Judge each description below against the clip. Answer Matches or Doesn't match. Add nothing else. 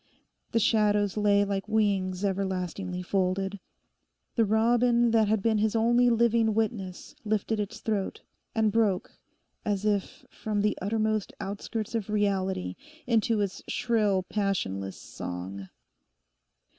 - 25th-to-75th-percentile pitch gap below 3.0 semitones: Matches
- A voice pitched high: Matches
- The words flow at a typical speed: Doesn't match